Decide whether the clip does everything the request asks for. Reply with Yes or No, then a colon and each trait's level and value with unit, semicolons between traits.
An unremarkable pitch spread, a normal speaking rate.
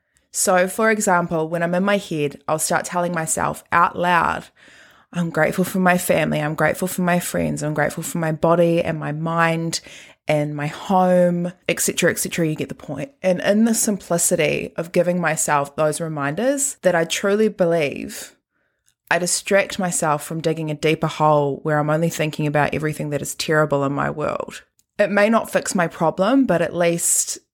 Yes: average, 3.1 semitones; average, 180 wpm